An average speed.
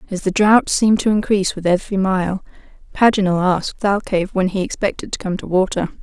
Yes: average, 190 wpm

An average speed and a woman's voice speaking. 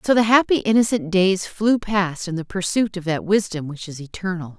No: fast, 210 wpm; female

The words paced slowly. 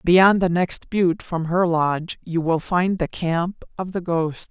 No: average, 200 wpm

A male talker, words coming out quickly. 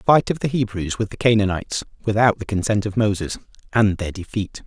No: male; average, 195 wpm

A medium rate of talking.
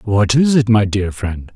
No: fast, 230 wpm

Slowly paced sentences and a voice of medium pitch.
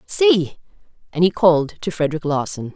Yes: slow, 130 wpm; medium, 155 Hz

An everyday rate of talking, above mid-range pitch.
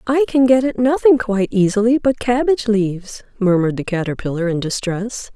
Yes: average, 170 wpm; high, 220 Hz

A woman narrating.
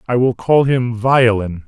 No: male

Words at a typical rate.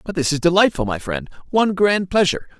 Yes: average, 185 wpm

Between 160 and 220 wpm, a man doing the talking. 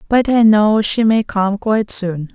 No: fast, 205 wpm; female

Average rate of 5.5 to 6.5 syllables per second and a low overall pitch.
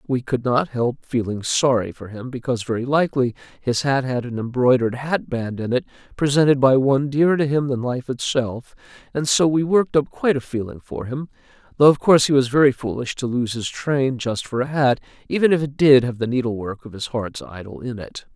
Yes: 5.6 syllables/s; low, 130 Hz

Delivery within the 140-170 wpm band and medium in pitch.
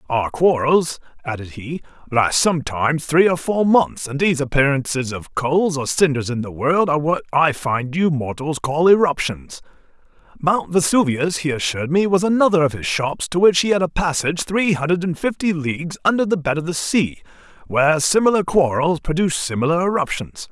No: average, 180 wpm; medium, 155 Hz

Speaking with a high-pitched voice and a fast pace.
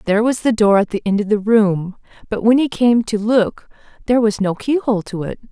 Yes: high, 215 Hz; fast, 250 wpm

